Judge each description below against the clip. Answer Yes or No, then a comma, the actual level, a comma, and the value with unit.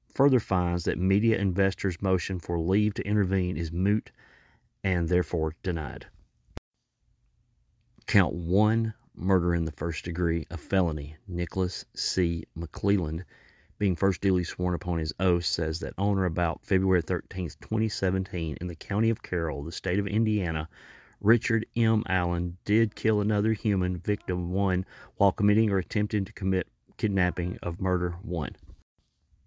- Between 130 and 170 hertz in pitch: No, very low, 95 Hz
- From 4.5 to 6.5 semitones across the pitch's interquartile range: No, average, 2.9 semitones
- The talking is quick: No, average, 145 wpm